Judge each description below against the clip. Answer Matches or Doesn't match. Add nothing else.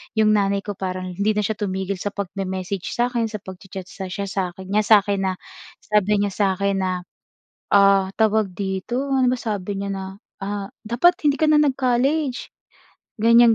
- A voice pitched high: Matches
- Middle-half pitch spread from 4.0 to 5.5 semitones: Doesn't match